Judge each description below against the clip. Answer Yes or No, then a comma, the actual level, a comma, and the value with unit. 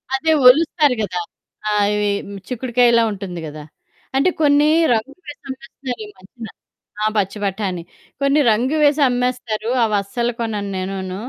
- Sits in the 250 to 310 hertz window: No, high, 230 Hz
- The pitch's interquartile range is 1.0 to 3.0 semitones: No, average, 5.1 semitones